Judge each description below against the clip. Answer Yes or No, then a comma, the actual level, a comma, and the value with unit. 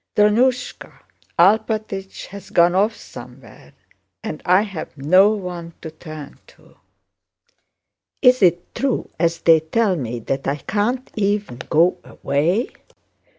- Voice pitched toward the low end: No, medium, 185 Hz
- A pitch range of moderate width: Yes, average, 4.6 semitones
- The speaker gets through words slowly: Yes, slow, 120 wpm